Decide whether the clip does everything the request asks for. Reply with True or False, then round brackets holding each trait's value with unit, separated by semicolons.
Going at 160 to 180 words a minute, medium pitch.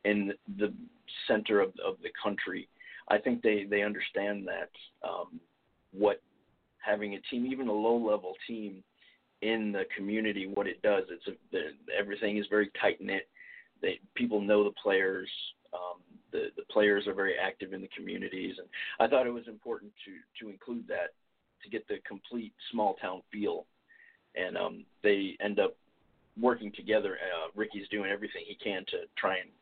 False (165 wpm; 105 Hz)